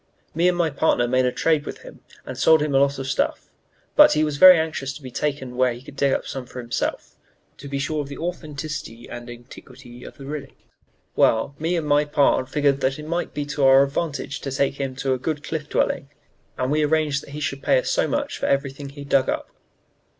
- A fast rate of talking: Yes, fast, 240 wpm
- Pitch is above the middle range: No, medium, 140 Hz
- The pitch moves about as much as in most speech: No, narrow, 2.3 semitones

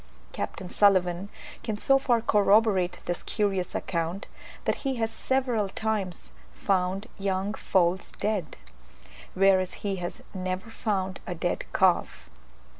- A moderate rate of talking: No, slow, 120 wpm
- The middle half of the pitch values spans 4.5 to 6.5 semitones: No, average, 2.7 semitones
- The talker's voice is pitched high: Yes, high, 195 Hz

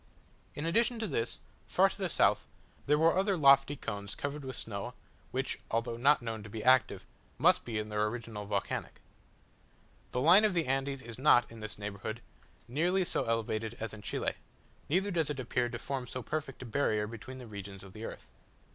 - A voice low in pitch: Yes, low, 120 Hz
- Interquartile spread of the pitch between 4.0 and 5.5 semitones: Yes, average, 4.9 semitones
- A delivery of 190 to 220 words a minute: Yes, average, 195 wpm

